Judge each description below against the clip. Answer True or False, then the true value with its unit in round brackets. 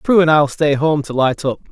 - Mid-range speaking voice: True (150 Hz)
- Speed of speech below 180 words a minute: False (280 wpm)